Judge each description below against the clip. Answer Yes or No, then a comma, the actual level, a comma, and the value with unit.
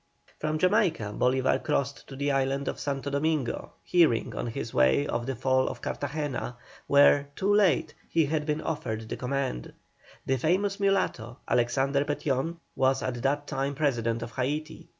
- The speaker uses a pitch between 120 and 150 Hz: Yes, medium, 140 Hz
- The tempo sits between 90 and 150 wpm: No, average, 160 wpm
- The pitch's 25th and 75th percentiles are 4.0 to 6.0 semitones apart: No, average, 3.2 semitones